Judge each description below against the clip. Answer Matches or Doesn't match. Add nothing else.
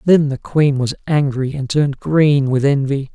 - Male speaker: Matches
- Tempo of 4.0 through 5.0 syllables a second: Matches